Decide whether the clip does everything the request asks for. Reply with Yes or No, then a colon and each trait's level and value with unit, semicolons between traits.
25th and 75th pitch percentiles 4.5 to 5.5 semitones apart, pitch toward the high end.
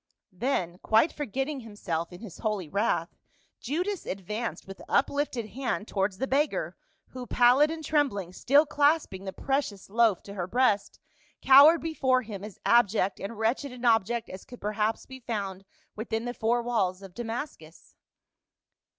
Yes: average, 5.2 semitones; high, 230 Hz